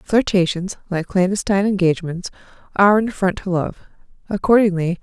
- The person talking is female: Yes, female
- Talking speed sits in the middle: No, slow, 120 wpm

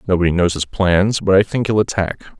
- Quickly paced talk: Yes, fast, 225 wpm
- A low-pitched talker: Yes, very low, 95 Hz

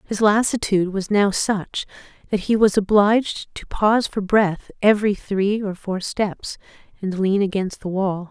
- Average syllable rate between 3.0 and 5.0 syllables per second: Yes, 4.5 syllables/s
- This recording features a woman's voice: Yes, female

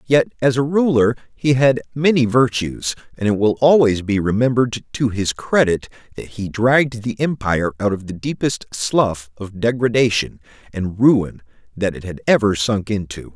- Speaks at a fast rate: No, average, 165 wpm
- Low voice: Yes, low, 115 Hz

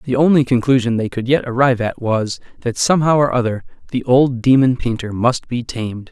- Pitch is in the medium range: No, low, 125 Hz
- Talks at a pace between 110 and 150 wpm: No, average, 195 wpm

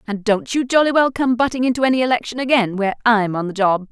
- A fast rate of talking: Yes, fast, 245 wpm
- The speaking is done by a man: No, female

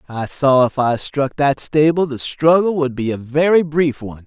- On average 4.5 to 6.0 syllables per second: Yes, 4.7 syllables/s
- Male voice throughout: Yes, male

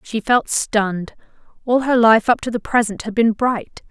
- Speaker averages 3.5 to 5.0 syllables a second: Yes, 4.6 syllables/s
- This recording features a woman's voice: Yes, female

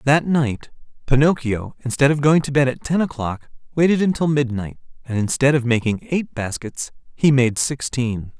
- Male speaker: Yes, male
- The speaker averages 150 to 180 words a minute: Yes, average, 165 wpm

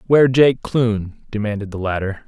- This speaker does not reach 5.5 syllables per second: Yes, 5.1 syllables/s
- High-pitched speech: No, low, 110 Hz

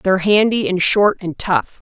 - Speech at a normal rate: Yes, average, 190 wpm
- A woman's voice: Yes, female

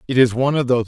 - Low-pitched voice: Yes, low, 125 Hz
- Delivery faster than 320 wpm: Yes, fast, 345 wpm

